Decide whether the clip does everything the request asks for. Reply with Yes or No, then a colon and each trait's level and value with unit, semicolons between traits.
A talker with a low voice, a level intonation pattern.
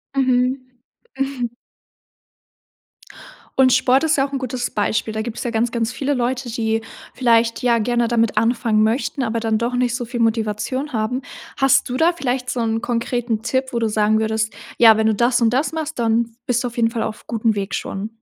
No: high, 235 Hz; narrow, 2.3 semitones